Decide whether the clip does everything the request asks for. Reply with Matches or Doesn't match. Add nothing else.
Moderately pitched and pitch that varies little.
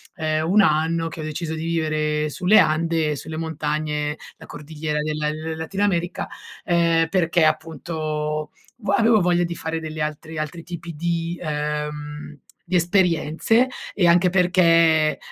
Matches